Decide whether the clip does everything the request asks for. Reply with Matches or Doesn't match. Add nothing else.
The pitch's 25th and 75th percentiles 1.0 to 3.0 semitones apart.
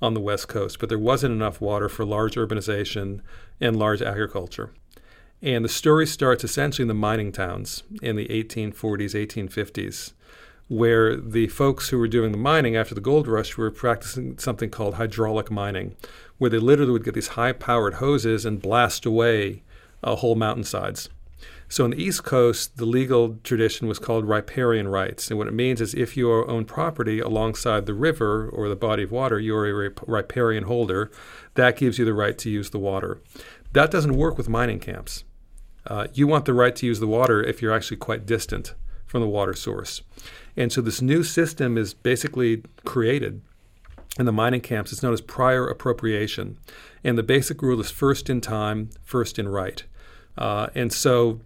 Matches